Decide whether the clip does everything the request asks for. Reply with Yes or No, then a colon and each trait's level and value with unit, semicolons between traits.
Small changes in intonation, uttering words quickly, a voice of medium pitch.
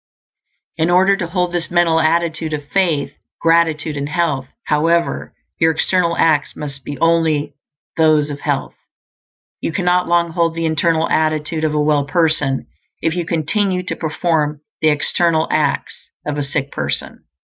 No: narrow, 2.2 semitones; average, 155 wpm; medium, 160 Hz